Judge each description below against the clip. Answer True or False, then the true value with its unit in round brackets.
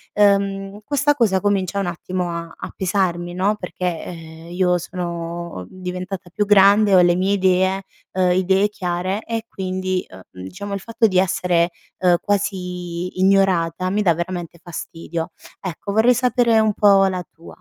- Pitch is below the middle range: False (185 Hz)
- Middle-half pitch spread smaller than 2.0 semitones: False (2.4 semitones)